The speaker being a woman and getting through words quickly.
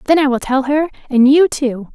Yes: female; fast, 245 wpm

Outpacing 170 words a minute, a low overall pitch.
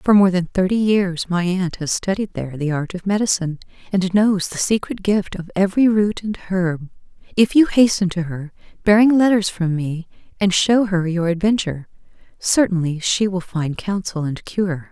No: average, 180 wpm; medium, 185 Hz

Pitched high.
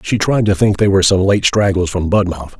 No: very low, 95 Hz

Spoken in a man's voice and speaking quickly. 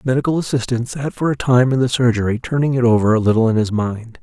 Yes: male; fast, 255 wpm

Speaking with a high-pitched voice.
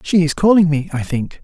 No: medium, 160 Hz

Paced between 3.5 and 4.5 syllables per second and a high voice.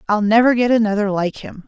No: 6.0 syllables/s; high, 215 Hz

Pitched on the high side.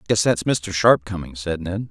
No: very low, 95 Hz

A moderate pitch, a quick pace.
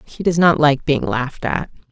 Yes: medium, 150 Hz; fast, 220 wpm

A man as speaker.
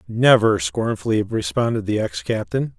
Yes: male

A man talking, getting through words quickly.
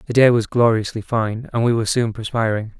Yes: male; fast, 215 wpm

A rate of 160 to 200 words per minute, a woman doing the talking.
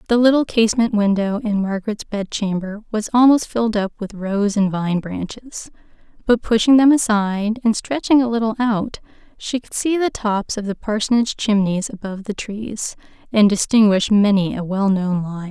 Yes: average, 180 wpm; female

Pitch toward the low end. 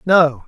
No: medium, 155 Hz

